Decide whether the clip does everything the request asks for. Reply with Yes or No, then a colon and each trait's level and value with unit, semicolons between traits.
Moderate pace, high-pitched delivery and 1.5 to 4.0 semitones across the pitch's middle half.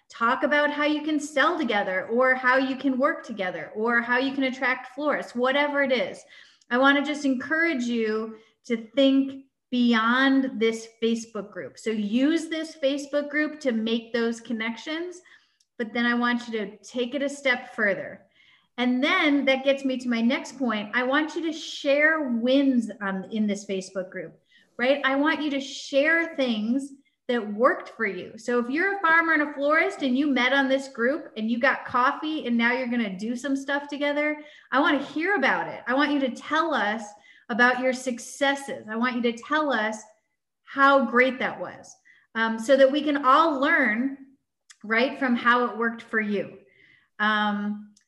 Yes: average, 190 wpm; very high, 260 Hz; average, 3.7 semitones